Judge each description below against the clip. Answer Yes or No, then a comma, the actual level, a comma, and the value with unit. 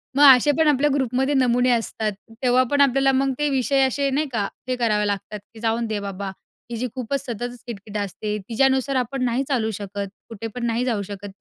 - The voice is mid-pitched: No, high, 245 Hz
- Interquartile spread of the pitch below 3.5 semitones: No, average, 3.8 semitones